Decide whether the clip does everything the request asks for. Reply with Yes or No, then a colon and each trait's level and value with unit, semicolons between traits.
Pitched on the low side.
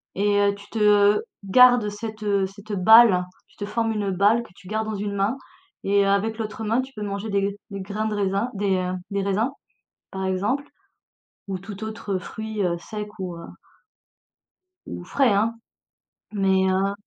No: high, 205 Hz